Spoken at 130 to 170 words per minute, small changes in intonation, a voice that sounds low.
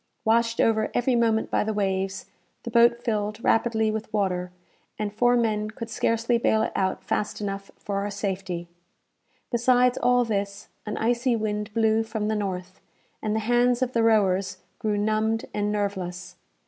No: average, 165 wpm; narrow, 2.3 semitones; high, 215 Hz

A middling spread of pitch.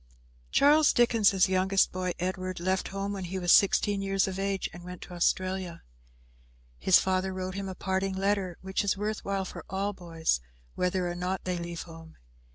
No: narrow, 1.4 semitones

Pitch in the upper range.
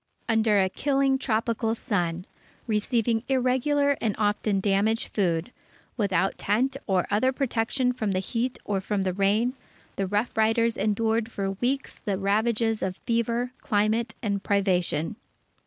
Yes: high, 220 Hz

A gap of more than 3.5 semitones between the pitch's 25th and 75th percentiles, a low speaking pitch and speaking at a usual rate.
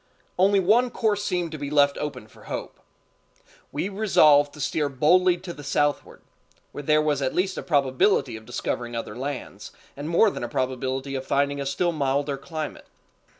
No: average, 4.3 semitones; medium, 145 Hz; average, 180 wpm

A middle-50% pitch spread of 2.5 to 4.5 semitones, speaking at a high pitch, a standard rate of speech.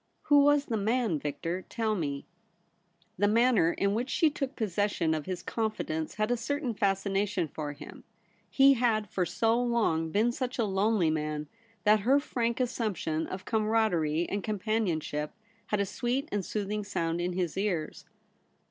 No: wide, 5.4 semitones; high, 205 Hz; average, 165 wpm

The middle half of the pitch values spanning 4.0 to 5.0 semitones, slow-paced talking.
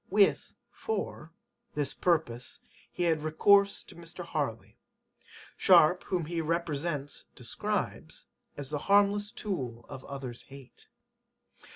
Yes: average, 4.6 semitones; slow, 110 wpm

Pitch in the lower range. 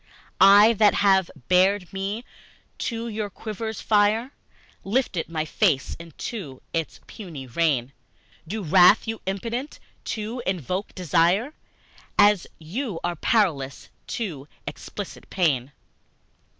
No: high, 195 Hz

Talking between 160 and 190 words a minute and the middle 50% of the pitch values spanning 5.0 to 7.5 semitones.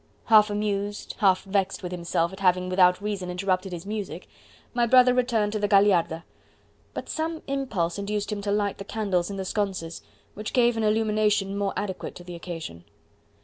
No: average, 180 wpm; narrow, 2.6 semitones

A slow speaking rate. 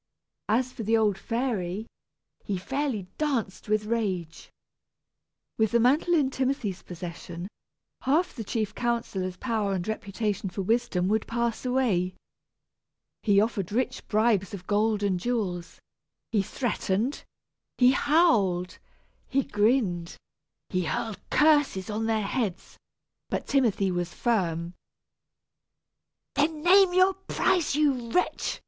Yes: slow, 120 wpm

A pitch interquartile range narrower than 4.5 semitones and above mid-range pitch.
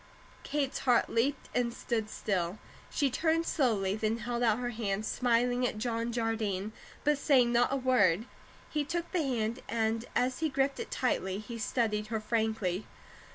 Yes: average, 3.0 semitones; high, 235 Hz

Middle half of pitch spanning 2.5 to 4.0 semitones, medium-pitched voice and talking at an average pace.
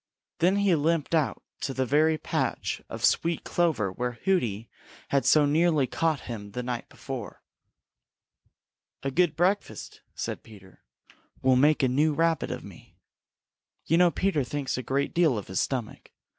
No: average, 5.0 semitones; medium, 145 Hz; average, 155 wpm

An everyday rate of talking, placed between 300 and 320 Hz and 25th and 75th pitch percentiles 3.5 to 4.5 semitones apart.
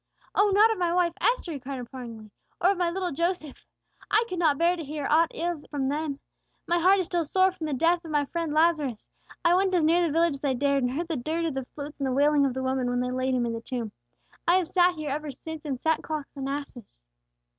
No: fast, 260 wpm; very high, 310 Hz; average, 4.2 semitones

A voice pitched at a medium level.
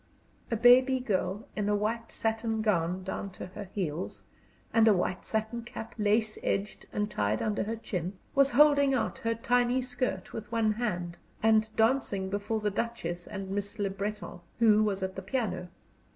No: high, 215 Hz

